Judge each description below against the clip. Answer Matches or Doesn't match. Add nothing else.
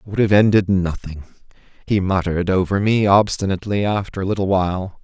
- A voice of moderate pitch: Doesn't match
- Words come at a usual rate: Matches